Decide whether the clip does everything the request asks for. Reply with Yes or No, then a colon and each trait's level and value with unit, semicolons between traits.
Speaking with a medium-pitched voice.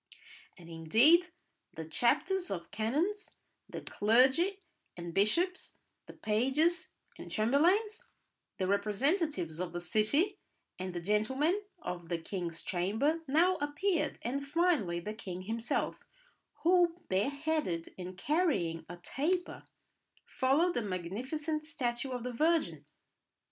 No: very high, 250 Hz